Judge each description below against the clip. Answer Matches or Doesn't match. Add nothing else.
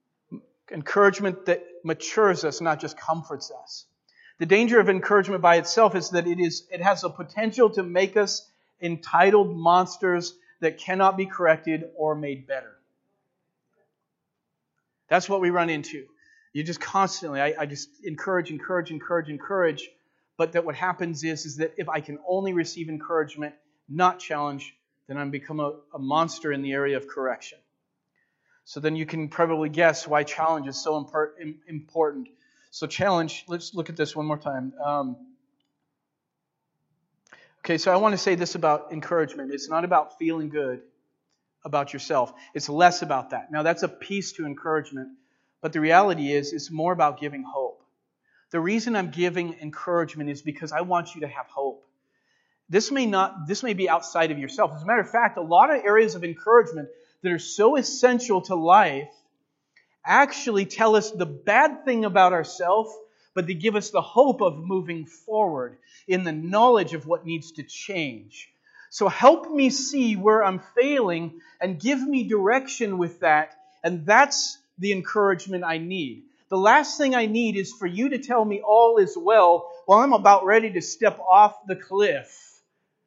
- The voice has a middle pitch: Matches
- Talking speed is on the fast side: Doesn't match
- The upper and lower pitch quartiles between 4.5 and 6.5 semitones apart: Matches